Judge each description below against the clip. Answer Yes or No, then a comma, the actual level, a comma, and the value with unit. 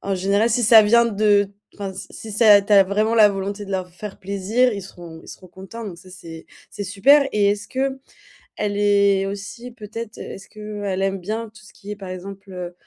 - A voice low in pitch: No, high, 205 Hz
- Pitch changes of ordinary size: No, narrow, 1.9 semitones